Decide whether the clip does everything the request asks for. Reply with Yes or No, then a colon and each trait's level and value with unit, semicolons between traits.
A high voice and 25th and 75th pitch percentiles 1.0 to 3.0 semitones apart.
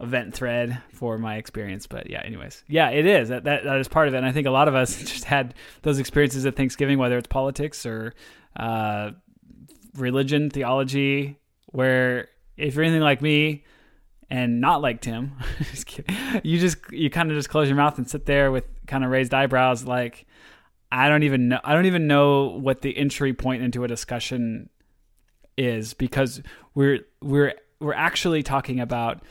No: low, 135 Hz; narrow, 2.6 semitones